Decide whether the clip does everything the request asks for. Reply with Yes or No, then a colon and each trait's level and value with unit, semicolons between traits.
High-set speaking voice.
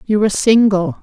Yes: high, 210 Hz